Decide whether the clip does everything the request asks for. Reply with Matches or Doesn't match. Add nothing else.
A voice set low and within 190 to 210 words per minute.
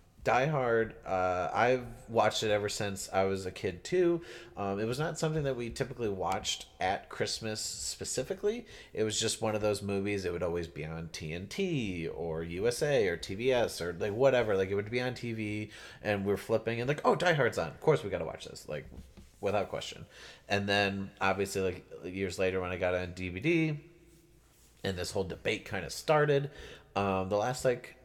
Matches